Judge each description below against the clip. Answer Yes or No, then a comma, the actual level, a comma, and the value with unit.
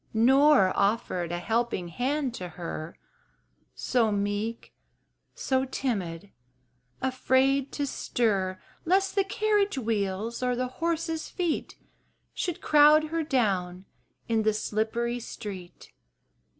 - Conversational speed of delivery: No, slow, 110 wpm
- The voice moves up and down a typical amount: No, wide, 6.4 semitones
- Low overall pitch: No, high, 235 Hz